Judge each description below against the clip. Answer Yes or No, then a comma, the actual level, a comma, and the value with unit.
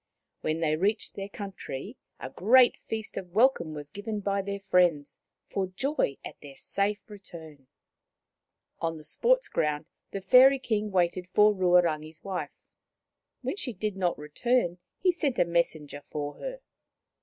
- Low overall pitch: No, high, 190 Hz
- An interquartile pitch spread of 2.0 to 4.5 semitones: No, average, 5.0 semitones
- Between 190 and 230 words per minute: No, average, 155 wpm